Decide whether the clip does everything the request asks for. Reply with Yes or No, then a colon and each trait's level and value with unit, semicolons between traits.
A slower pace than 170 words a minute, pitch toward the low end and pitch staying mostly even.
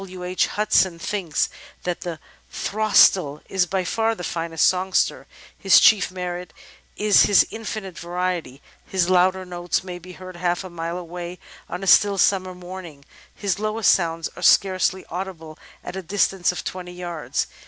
No: average, 160 wpm; medium, 180 Hz; narrow, 1.7 semitones